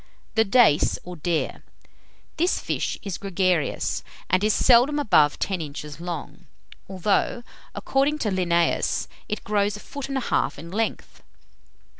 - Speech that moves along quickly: No, average, 140 wpm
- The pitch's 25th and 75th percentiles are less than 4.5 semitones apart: No, wide, 5.6 semitones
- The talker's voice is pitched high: Yes, high, 195 Hz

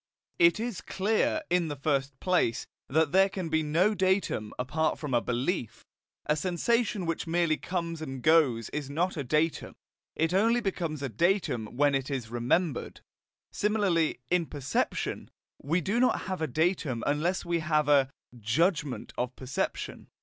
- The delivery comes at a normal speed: Yes, average, 155 wpm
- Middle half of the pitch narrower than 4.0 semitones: No, average, 4.9 semitones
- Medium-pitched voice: Yes, medium, 160 Hz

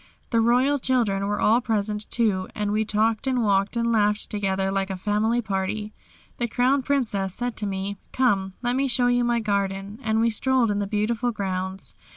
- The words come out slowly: No, average, 190 wpm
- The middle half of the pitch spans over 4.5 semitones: No, average, 3.3 semitones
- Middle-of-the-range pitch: No, high, 215 Hz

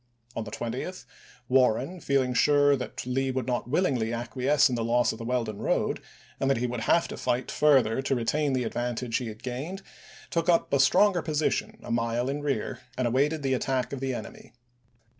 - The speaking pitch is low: Yes, low, 130 Hz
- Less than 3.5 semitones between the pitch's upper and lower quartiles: Yes, average, 3.0 semitones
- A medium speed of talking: Yes, average, 195 wpm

